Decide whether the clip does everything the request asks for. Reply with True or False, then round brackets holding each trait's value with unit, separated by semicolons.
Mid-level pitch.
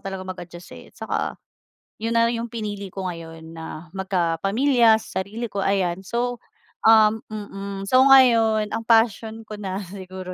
False (200 Hz)